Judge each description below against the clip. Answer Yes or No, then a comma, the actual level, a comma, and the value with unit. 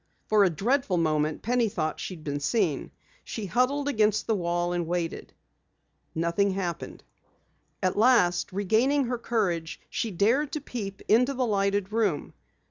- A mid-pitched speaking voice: No, high, 200 Hz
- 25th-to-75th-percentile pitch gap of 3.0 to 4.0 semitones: No, average, 5.3 semitones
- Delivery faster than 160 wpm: No, average, 155 wpm